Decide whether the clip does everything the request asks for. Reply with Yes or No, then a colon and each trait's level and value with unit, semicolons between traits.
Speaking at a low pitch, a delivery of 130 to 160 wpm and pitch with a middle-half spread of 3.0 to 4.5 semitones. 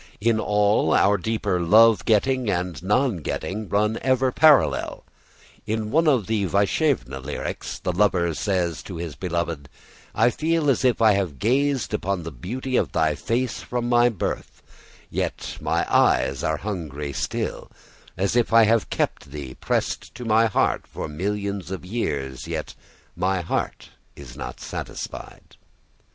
No: low, 100 Hz; average, 150 wpm; average, 5.3 semitones